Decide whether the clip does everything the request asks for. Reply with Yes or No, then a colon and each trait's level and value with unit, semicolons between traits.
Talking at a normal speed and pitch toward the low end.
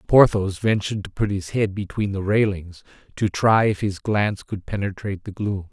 Yes: average, 190 wpm; low, 100 Hz